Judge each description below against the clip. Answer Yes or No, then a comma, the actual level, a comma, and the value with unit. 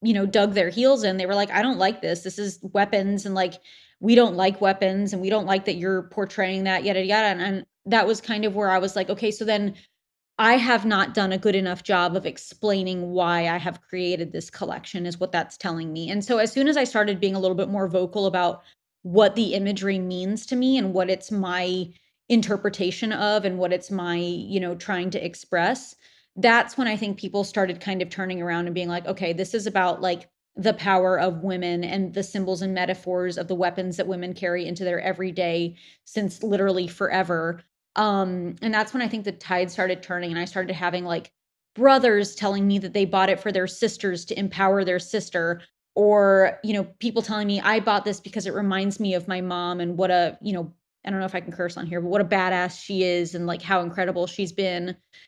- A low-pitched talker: No, high, 190 Hz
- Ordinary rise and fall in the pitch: No, narrow, 2.1 semitones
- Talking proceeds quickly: Yes, fast, 230 wpm